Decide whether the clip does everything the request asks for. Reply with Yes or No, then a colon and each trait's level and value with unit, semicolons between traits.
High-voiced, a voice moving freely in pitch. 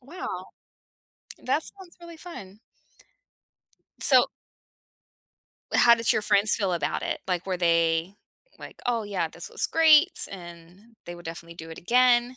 Yes: high, 205 Hz; wide, 6.6 semitones